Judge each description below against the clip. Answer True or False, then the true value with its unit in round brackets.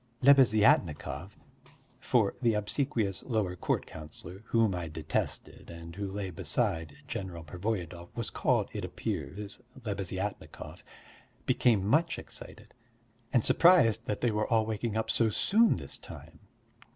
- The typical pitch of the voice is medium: False (105 Hz)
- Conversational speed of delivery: False (125 wpm)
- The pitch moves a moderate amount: True (4.2 semitones)